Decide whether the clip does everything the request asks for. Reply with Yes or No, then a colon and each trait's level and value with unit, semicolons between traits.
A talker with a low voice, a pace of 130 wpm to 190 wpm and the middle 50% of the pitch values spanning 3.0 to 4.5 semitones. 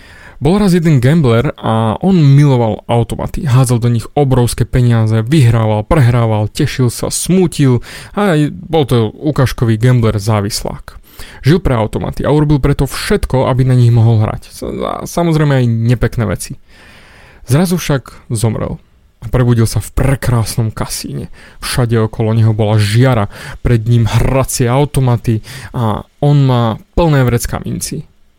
Yes: low, 125 Hz; average, 135 wpm; average, 4.0 semitones